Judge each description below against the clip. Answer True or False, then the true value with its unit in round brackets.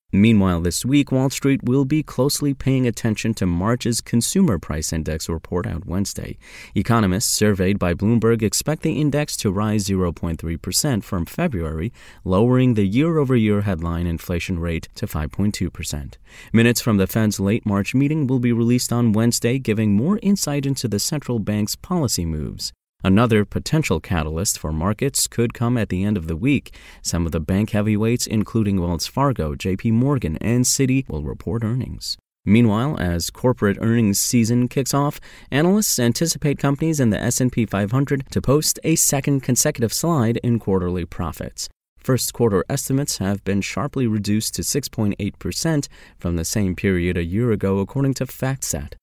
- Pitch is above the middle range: False (110 Hz)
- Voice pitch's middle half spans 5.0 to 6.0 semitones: True (5.4 semitones)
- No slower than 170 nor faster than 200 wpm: False (160 wpm)